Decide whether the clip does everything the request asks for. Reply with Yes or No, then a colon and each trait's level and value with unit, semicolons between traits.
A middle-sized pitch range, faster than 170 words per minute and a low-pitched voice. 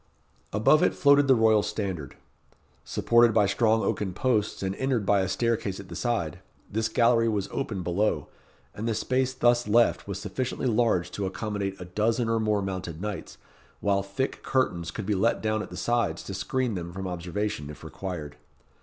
Yes: average, 3.6 semitones; average, 180 wpm; low, 105 Hz